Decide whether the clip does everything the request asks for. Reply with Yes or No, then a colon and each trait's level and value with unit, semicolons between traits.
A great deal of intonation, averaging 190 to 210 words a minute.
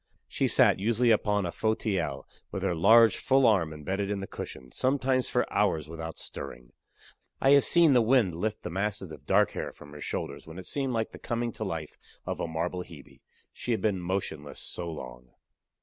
Yes: wide, 6.0 semitones; average, 195 wpm